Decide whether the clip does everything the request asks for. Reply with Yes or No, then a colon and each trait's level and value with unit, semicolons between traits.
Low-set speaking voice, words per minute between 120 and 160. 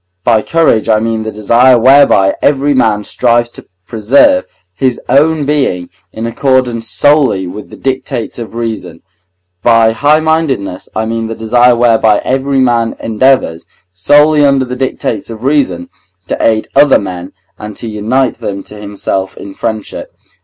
Yes: low, 115 Hz; average, 150 wpm